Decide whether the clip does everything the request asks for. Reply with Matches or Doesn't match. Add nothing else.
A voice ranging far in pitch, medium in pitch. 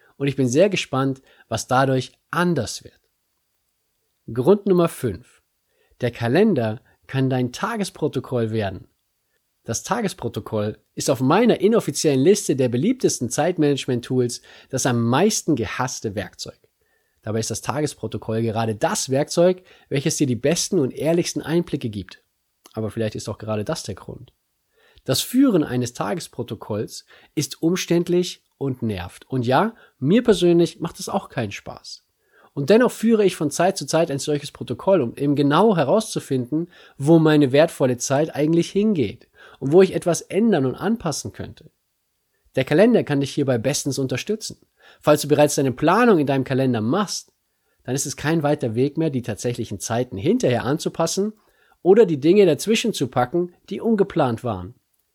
Matches